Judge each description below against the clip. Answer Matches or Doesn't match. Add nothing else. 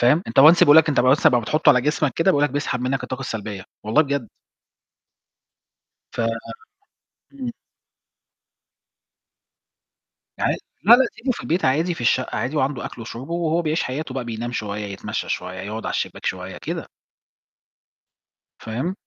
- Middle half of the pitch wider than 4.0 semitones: Matches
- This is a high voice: Doesn't match